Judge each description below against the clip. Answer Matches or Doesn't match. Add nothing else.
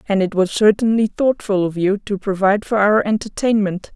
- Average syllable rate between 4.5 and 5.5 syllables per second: Matches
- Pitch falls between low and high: Doesn't match